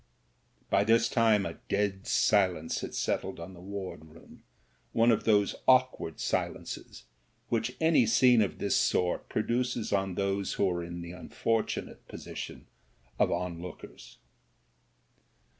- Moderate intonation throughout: Yes, average, 4.1 semitones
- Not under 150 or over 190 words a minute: No, average, 140 wpm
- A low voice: Yes, low, 100 Hz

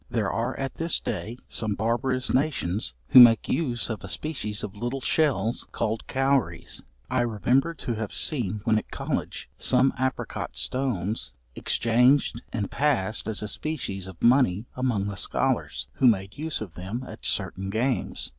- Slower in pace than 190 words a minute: Yes, average, 160 wpm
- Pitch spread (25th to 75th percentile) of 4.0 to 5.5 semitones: Yes, average, 4.3 semitones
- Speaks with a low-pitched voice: Yes, low, 115 Hz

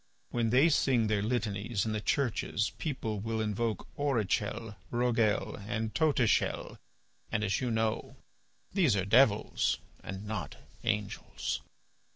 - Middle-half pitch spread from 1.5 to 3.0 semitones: Yes, narrow, 2.6 semitones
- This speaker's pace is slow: Yes, slow, 125 wpm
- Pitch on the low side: Yes, low, 110 Hz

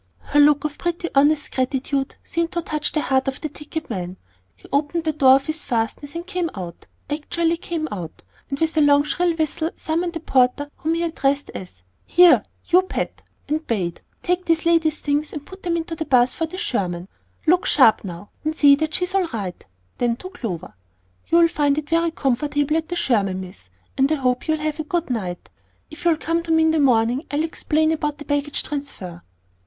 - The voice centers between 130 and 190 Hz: No, very high, 300 Hz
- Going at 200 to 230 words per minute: Yes, fast, 205 wpm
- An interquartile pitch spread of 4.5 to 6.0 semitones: No, average, 4.0 semitones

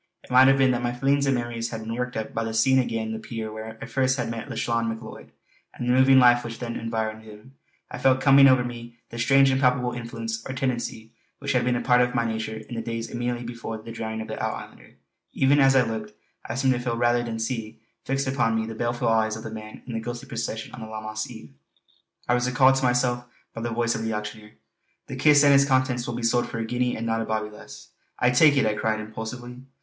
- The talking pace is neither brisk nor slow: No, fast, 255 wpm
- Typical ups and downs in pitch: No, narrow, 2.1 semitones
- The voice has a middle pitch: No, low, 120 Hz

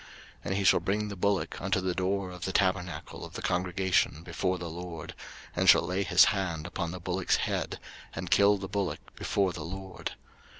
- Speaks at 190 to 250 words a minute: Yes, average, 200 wpm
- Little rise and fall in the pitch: Yes, narrow, 1.7 semitones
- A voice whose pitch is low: Yes, very low, 95 Hz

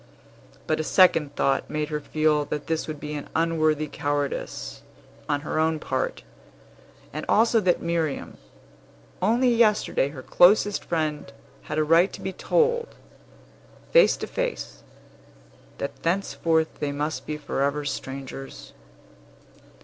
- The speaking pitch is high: No, medium, 155 Hz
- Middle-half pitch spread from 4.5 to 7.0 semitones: No, average, 3.6 semitones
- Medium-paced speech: No, slow, 130 wpm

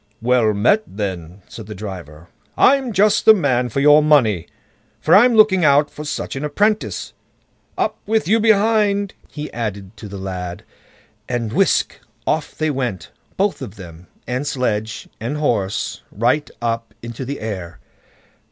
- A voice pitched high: No, low, 125 Hz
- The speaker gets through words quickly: No, average, 150 wpm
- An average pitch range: No, wide, 7.5 semitones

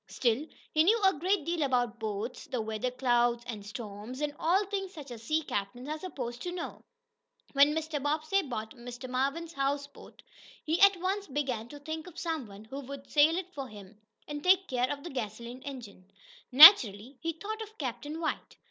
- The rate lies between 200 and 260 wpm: No, average, 190 wpm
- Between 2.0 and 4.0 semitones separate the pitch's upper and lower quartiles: No, average, 5.3 semitones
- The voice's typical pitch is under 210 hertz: No, very high, 280 Hz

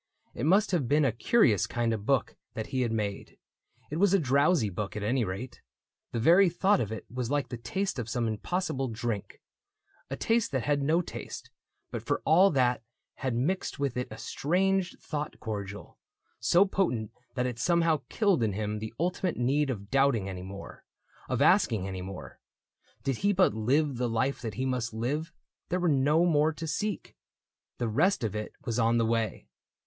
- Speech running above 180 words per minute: Yes, average, 200 wpm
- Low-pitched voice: Yes, low, 130 Hz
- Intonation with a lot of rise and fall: Yes, wide, 6.6 semitones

